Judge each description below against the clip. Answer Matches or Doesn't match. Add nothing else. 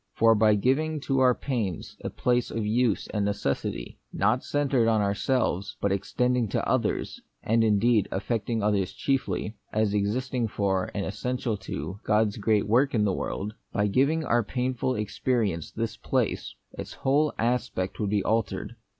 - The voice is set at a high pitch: Doesn't match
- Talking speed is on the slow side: Doesn't match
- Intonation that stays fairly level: Doesn't match